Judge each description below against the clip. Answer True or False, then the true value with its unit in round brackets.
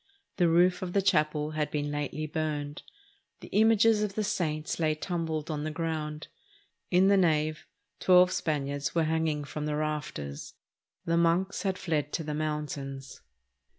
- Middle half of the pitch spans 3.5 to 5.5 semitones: False (2.8 semitones)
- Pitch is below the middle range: False (155 Hz)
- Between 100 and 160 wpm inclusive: True (155 wpm)